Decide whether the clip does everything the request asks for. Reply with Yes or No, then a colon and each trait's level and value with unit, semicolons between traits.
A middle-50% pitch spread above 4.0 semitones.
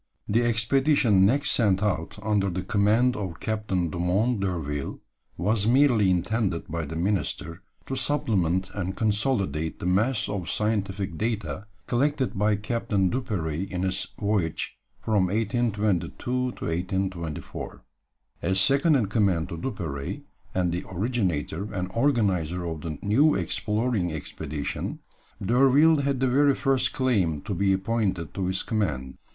Yes: average, 4.7 semitones